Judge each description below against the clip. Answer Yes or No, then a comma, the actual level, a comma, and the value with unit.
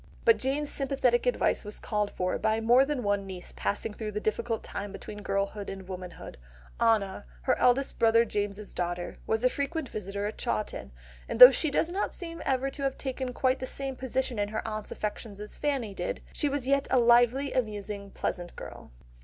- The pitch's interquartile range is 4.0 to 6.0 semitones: Yes, average, 4.6 semitones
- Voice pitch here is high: Yes, high, 225 Hz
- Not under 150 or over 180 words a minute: No, average, 195 wpm